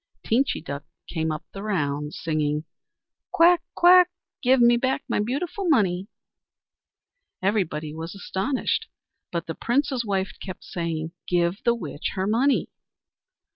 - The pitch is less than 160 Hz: No, high, 195 Hz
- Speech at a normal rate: No, slow, 130 wpm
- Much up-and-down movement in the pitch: Yes, wide, 7.5 semitones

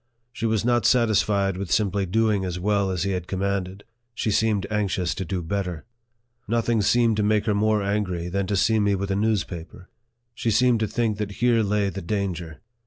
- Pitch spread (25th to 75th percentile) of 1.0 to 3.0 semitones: Yes, narrow, 2.4 semitones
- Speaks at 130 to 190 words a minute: No, average, 200 wpm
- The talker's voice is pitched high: No, low, 100 Hz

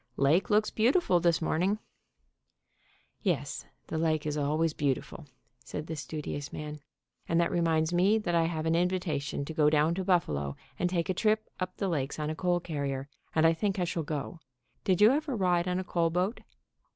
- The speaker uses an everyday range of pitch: Yes, average, 3.2 semitones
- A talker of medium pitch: Yes, medium, 165 Hz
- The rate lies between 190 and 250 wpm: Yes, average, 200 wpm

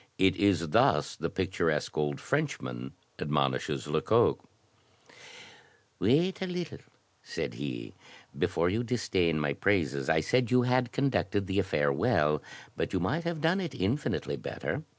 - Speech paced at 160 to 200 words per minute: No, average, 140 wpm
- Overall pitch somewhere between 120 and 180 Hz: No, very low, 95 Hz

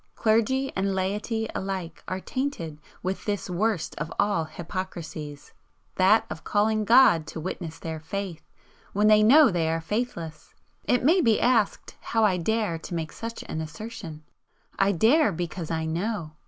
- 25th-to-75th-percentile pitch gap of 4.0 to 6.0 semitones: Yes, average, 5.1 semitones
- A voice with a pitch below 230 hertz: Yes, high, 190 Hz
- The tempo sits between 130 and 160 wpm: Yes, average, 155 wpm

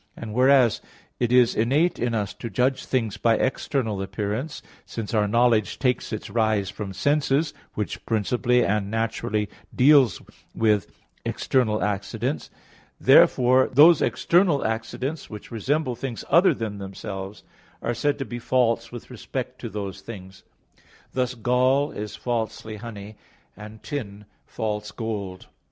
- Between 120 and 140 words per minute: Yes, slow, 135 wpm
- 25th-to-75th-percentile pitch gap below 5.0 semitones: Yes, average, 3.5 semitones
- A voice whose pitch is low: Yes, low, 115 Hz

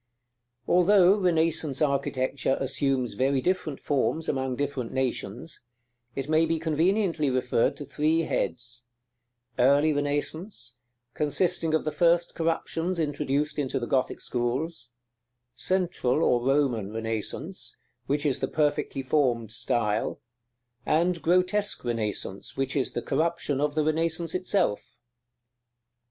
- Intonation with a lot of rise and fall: No, average, 4.3 semitones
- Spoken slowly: Yes, slow, 120 wpm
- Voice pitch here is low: No, medium, 145 Hz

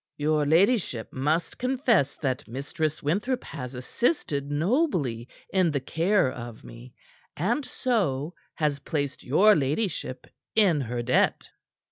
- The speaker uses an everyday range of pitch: No, wide, 7.2 semitones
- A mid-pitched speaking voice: Yes, medium, 150 Hz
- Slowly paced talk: Yes, slow, 120 wpm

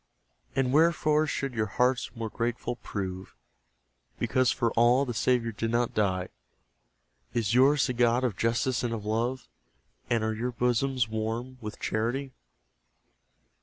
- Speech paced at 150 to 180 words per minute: No, average, 140 wpm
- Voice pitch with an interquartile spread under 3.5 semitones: Yes, narrow, 2.5 semitones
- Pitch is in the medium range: No, low, 120 Hz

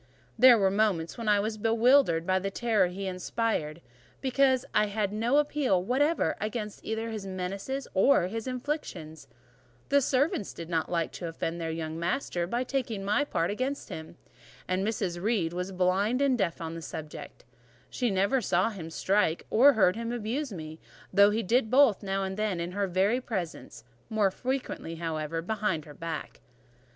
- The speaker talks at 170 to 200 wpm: Yes, average, 175 wpm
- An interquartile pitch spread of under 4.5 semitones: No, wide, 5.4 semitones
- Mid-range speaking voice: No, high, 200 Hz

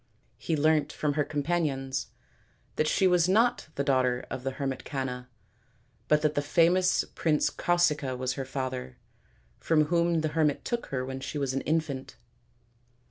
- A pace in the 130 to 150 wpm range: No, average, 160 wpm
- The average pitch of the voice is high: No, medium, 145 Hz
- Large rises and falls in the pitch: No, average, 3.5 semitones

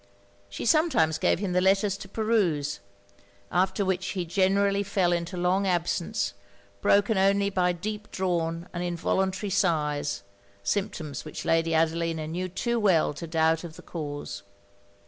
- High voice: No, medium, 180 Hz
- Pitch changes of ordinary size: Yes, average, 3.2 semitones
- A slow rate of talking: No, average, 145 wpm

